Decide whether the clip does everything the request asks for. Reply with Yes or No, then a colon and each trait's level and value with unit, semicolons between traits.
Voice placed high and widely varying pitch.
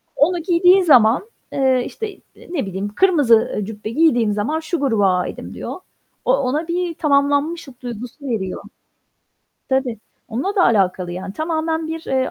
Yes: very high, 275 Hz; wide, 6.7 semitones